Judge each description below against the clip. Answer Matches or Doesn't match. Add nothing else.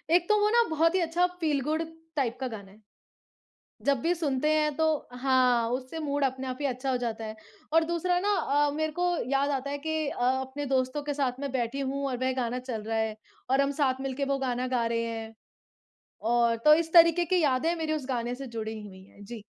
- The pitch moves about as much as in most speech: Matches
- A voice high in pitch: Matches